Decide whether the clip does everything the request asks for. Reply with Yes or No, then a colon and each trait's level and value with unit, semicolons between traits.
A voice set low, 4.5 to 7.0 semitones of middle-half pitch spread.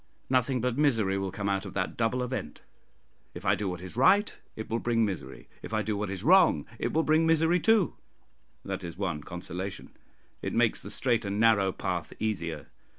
Yes: low, 105 Hz; average, 5.2 semitones